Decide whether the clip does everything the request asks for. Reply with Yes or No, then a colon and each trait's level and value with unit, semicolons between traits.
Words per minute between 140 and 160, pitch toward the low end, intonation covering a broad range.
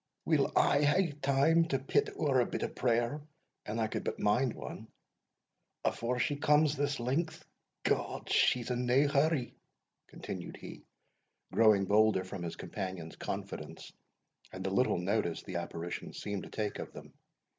Yes: average, 155 wpm; low, 120 Hz; wide, 5.9 semitones